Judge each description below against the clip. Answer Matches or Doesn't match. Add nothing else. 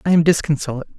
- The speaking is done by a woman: Doesn't match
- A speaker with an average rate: Matches